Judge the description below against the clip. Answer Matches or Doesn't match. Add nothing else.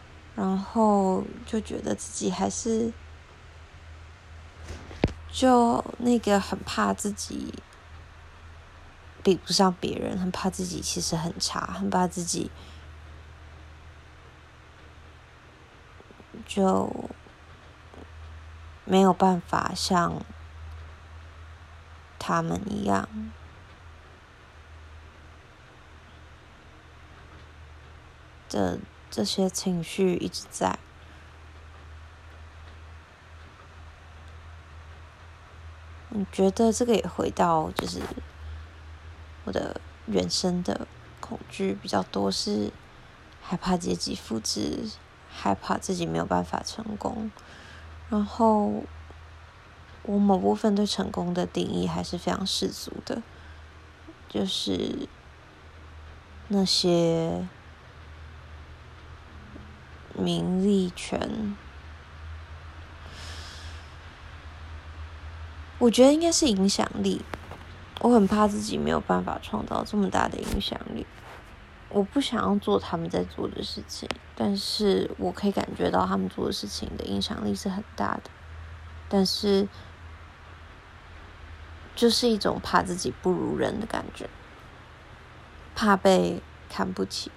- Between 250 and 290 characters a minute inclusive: Doesn't match